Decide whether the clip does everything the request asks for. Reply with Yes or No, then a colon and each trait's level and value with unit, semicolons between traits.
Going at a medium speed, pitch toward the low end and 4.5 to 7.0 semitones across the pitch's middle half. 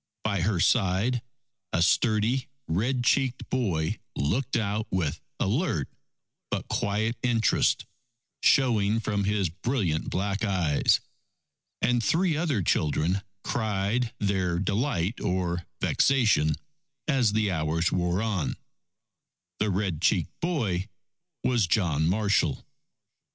No: slow, 110 wpm; low, 100 Hz; average, 5.0 semitones